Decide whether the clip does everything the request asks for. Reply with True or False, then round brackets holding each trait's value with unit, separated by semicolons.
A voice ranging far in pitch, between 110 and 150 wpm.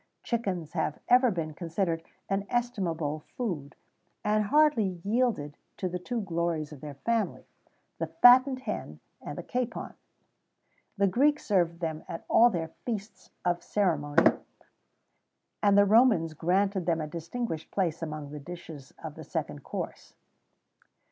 True (6.0 semitones; 140 wpm)